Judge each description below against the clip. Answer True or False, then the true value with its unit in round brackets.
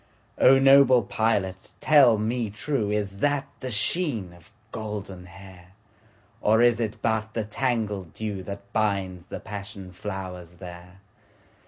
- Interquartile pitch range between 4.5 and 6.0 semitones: False (3.3 semitones)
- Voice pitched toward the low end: True (105 Hz)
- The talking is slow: True (120 wpm)